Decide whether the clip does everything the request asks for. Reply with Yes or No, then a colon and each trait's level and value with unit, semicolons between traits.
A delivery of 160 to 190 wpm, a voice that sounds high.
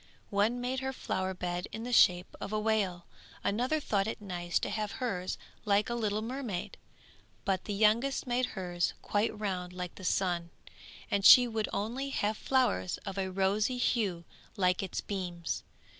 Yes: average, 170 wpm; high, 205 Hz